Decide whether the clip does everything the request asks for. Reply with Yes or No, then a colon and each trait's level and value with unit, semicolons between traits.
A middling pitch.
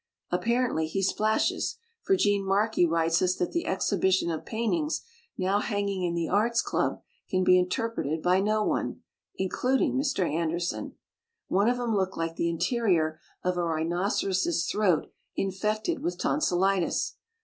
No: high, 195 Hz